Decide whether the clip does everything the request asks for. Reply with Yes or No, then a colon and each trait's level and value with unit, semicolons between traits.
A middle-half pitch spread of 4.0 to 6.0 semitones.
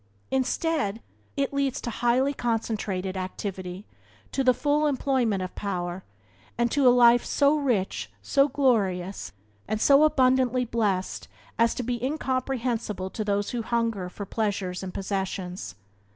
Yes: average, 5.3 semitones